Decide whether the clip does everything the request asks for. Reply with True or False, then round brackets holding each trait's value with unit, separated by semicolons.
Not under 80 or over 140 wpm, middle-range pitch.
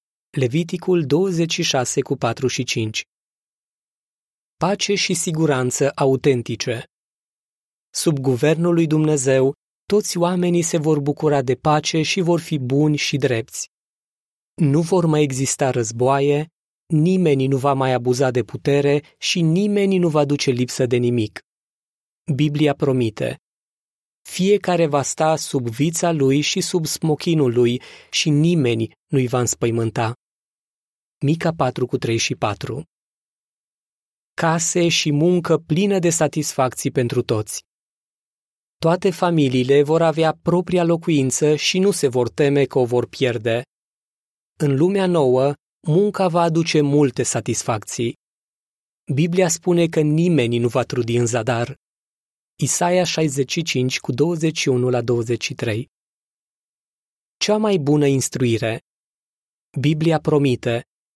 True (115 wpm; 145 Hz)